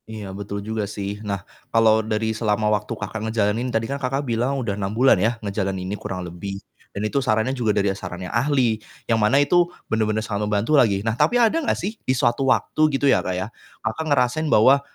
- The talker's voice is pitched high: No, low, 110 Hz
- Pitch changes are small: No, average, 4.0 semitones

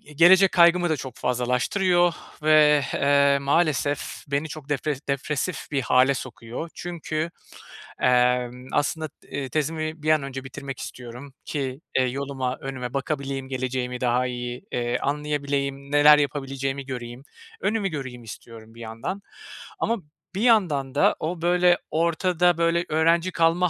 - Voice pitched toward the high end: No, medium, 140 Hz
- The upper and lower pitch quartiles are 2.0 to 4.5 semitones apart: Yes, average, 3.8 semitones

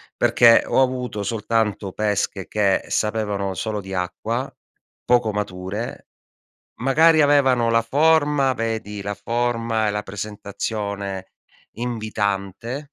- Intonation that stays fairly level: No, average, 3.1 semitones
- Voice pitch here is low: Yes, low, 110 Hz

